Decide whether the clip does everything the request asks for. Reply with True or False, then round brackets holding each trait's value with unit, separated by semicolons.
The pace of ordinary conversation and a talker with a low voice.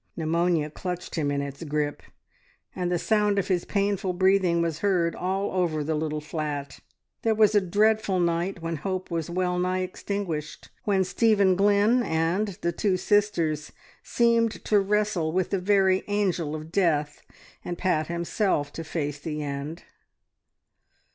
False (155 wpm; 180 Hz)